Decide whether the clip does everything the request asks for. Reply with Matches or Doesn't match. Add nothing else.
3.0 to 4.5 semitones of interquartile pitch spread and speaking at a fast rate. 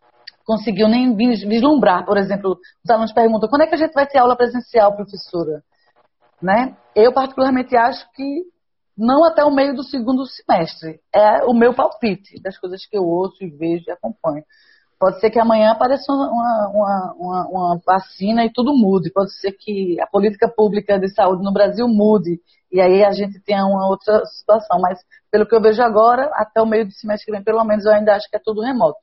Matches